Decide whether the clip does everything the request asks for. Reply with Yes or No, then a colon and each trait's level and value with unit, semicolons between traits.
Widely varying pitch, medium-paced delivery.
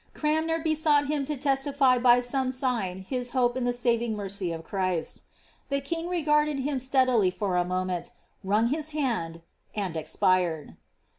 Yes: wide, 7.0 semitones; average, 155 wpm